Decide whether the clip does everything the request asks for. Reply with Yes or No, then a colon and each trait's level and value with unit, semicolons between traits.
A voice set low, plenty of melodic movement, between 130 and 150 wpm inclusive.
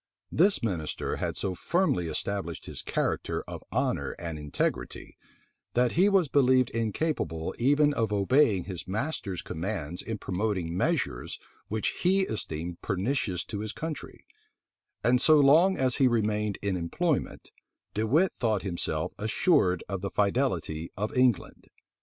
Yes: low, 110 Hz; wide, 7.1 semitones; average, 140 wpm